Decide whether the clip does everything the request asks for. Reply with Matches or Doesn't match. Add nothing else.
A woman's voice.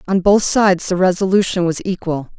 Matches